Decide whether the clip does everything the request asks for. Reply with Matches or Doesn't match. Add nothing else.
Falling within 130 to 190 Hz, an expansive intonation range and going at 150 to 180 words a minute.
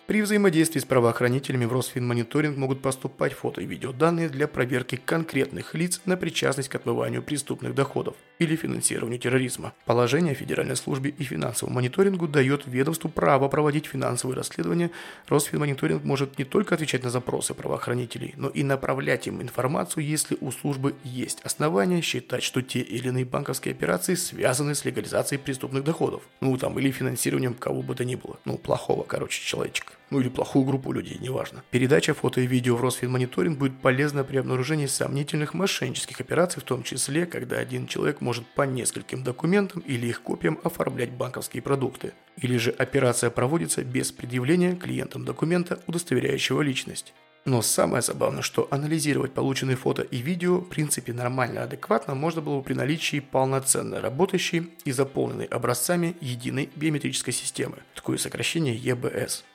Doesn't match